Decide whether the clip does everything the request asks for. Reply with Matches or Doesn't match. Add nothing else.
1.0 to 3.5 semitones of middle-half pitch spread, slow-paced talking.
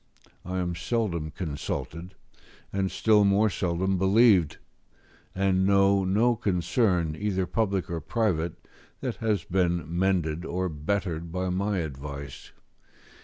Matches